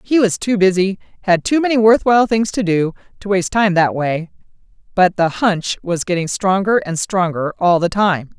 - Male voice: No, female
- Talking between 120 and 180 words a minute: No, average, 195 wpm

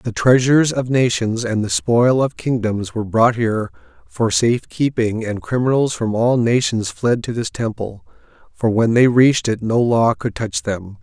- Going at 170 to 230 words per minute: Yes, average, 185 wpm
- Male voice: Yes, male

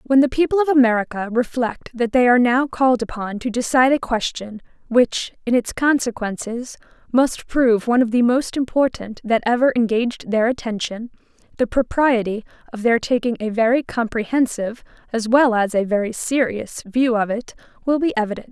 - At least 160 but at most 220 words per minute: Yes, average, 170 wpm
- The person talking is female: Yes, female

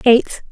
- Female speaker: Yes, female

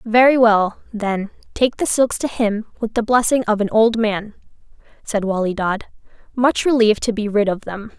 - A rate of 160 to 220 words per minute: Yes, average, 190 wpm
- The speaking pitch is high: Yes, high, 220 Hz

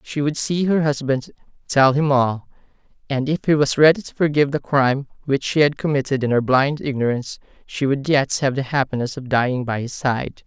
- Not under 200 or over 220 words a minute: Yes, fast, 205 wpm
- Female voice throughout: No, male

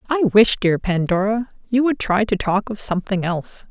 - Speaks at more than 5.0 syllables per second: No, 4.9 syllables/s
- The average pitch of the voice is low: No, high, 205 Hz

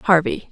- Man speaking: No, female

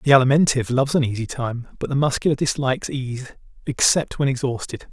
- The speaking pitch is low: Yes, low, 130 Hz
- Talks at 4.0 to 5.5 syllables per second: No, 6.2 syllables/s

